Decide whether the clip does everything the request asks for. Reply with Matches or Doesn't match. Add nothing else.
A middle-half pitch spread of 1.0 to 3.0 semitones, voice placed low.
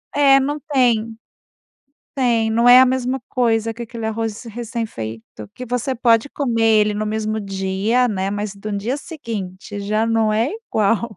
Doesn't match